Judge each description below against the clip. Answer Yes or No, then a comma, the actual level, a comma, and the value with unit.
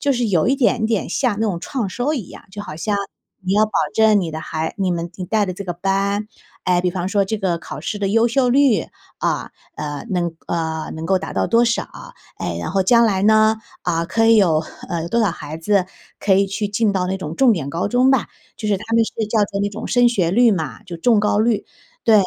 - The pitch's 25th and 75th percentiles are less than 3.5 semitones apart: No, average, 4.1 semitones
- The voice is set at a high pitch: Yes, high, 200 Hz